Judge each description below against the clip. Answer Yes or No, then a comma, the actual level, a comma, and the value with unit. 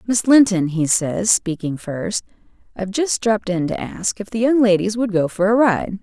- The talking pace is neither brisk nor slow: No, fast, 210 wpm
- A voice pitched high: Yes, high, 200 Hz